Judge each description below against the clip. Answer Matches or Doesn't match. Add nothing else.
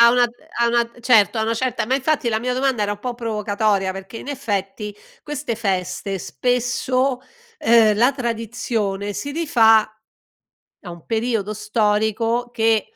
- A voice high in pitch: Matches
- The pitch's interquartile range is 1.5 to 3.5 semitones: Matches